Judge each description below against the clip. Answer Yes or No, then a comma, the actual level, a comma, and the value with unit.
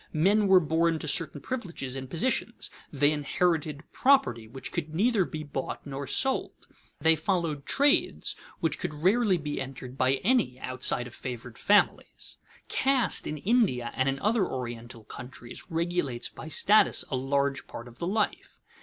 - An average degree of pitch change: No, wide, 6.2 semitones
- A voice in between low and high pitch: Yes, medium, 155 Hz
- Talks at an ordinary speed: Yes, average, 155 wpm